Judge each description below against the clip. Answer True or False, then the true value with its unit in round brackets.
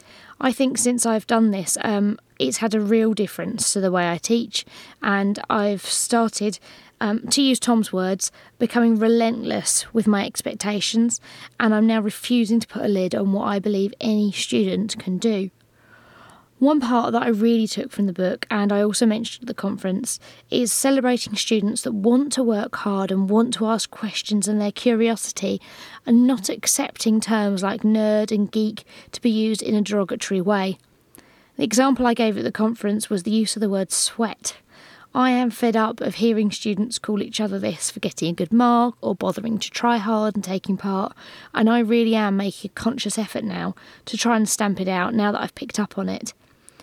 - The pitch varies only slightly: True (2.3 semitones)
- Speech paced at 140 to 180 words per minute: False (195 wpm)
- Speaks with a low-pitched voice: False (220 Hz)